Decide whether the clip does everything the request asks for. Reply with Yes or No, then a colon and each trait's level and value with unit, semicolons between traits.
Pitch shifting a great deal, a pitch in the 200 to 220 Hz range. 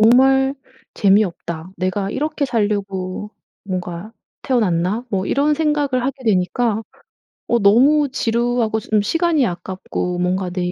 Yes: wide, 5.9 semitones; high, 215 Hz